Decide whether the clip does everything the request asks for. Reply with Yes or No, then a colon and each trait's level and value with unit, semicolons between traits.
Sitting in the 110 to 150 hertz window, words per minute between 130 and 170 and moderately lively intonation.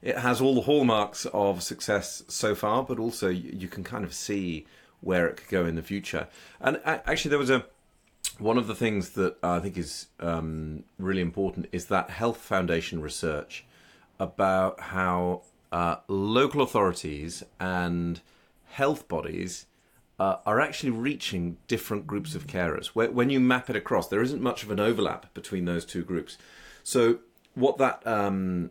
No: very low, 95 Hz; average, 165 wpm; average, 4.8 semitones